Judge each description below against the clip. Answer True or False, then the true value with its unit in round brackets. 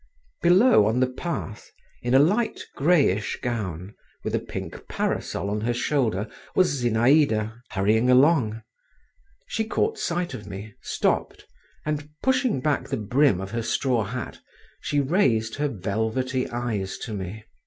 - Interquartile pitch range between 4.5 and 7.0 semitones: True (5.5 semitones)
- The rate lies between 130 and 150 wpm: True (145 wpm)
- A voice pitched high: False (120 Hz)